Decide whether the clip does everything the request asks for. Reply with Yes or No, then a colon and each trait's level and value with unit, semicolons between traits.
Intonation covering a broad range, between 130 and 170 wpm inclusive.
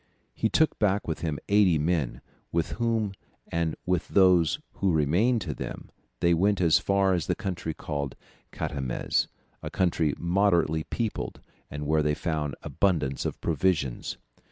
No: average, 4.2 semitones; average, 150 wpm